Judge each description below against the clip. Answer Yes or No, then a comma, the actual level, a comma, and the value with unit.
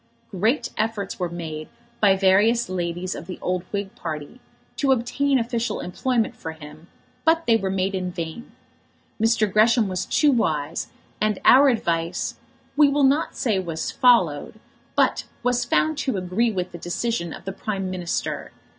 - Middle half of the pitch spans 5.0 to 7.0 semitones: Yes, average, 5.3 semitones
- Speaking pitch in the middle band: No, high, 200 Hz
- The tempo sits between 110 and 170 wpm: Yes, average, 160 wpm